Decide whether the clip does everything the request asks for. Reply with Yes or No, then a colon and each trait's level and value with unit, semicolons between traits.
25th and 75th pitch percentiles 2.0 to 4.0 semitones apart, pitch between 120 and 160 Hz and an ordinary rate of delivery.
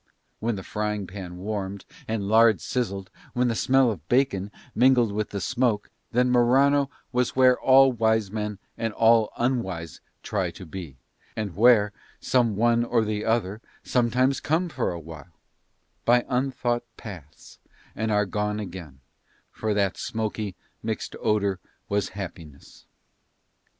No: average, 3.6 semitones; low, 110 Hz; average, 145 wpm